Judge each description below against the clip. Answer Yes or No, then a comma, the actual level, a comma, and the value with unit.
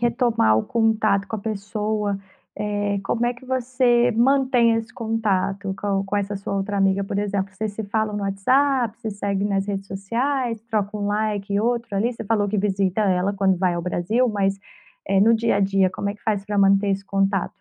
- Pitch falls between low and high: No, high, 205 Hz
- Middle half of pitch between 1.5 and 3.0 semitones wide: Yes, narrow, 2.5 semitones